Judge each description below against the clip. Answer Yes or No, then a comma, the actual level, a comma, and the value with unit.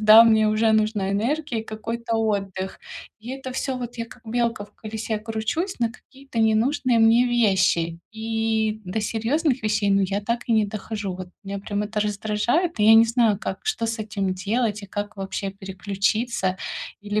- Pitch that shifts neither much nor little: No, narrow, 2.3 semitones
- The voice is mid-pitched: No, high, 220 Hz